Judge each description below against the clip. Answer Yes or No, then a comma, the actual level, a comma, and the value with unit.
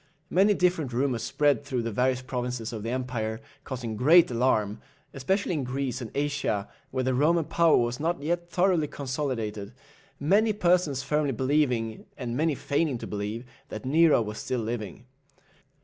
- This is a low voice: Yes, low, 130 Hz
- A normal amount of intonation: Yes, average, 4.5 semitones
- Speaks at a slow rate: No, average, 160 wpm